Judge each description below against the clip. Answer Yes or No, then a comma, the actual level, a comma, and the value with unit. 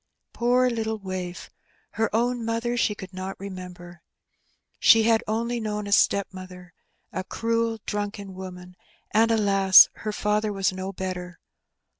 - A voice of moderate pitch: No, high, 205 Hz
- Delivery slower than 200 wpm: Yes, average, 140 wpm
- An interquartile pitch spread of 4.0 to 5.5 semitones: No, average, 3.2 semitones